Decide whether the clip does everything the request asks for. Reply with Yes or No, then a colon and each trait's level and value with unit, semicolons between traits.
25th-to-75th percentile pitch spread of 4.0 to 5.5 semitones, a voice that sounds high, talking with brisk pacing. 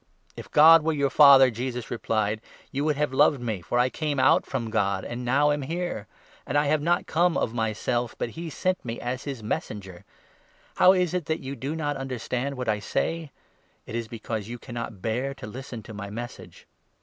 No: average, 4.6 semitones; low, 130 Hz; fast, 215 wpm